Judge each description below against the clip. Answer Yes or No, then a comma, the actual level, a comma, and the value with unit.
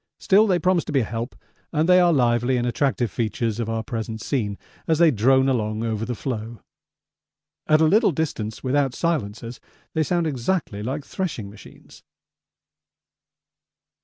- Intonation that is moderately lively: No, wide, 5.8 semitones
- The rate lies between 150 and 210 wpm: Yes, average, 160 wpm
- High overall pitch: No, low, 125 Hz